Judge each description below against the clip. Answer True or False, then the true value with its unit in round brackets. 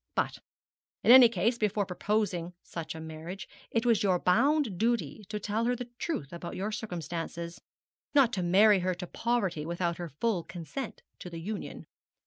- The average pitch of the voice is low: False (195 Hz)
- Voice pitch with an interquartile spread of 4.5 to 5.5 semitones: True (4.8 semitones)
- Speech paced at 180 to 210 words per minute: False (170 wpm)